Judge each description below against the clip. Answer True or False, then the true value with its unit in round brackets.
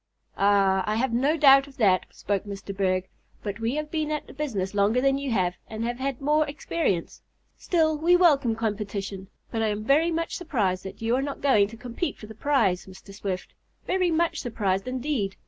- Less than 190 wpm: False (200 wpm)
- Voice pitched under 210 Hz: False (230 Hz)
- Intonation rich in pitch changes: True (6.3 semitones)